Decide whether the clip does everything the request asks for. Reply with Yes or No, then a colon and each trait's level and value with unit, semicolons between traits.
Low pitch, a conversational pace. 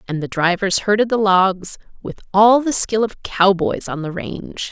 No: high, 200 Hz; average, 190 wpm